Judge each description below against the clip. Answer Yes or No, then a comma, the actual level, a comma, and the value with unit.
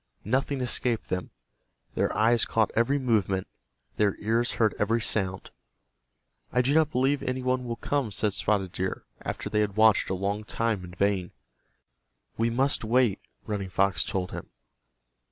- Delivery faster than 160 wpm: No, average, 155 wpm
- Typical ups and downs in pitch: Yes, average, 4.1 semitones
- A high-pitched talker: No, low, 110 Hz